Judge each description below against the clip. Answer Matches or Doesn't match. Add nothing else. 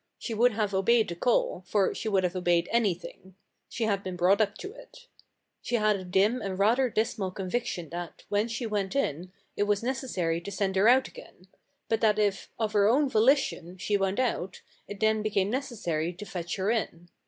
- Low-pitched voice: Doesn't match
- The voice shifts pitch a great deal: Doesn't match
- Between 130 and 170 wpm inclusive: Doesn't match